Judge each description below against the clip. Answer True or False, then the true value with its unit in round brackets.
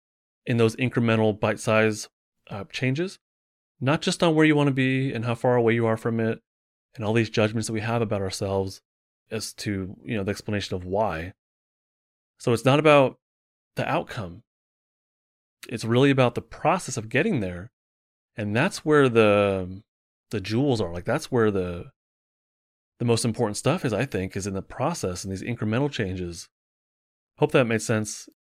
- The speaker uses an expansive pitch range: False (4.5 semitones)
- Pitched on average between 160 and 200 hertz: False (110 Hz)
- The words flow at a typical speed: True (175 wpm)